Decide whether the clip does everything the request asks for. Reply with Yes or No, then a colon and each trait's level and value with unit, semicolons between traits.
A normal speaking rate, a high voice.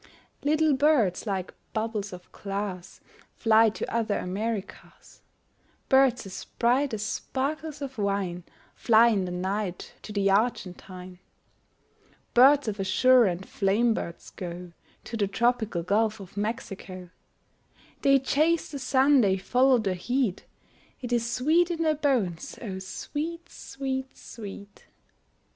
No: slow, 130 wpm; high, 220 Hz